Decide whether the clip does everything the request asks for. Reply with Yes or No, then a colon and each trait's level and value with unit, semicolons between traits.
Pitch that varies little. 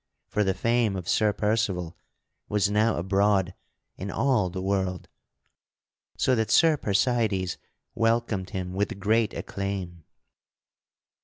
No: average, 3.1 semitones